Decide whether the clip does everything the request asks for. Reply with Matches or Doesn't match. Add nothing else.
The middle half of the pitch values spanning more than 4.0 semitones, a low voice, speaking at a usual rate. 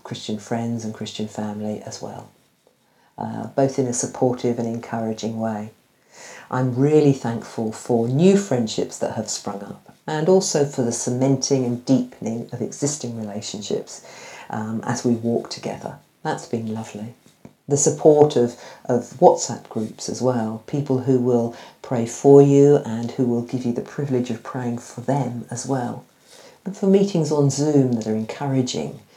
Doesn't match